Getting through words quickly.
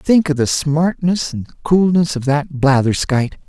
No: average, 155 wpm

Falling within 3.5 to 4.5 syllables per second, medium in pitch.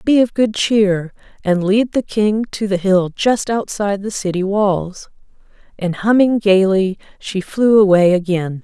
No: 4.1 syllables/s; high, 200 Hz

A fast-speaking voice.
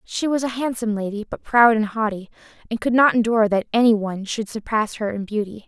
Yes: fast, 220 wpm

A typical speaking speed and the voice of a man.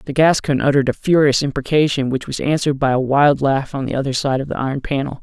No: fast, 240 wpm; male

